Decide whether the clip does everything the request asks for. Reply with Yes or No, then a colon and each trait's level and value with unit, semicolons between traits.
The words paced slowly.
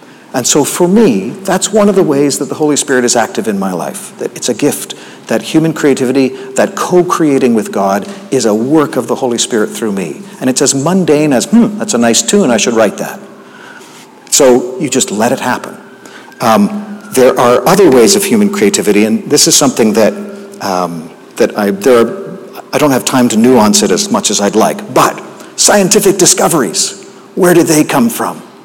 No: fast, 205 wpm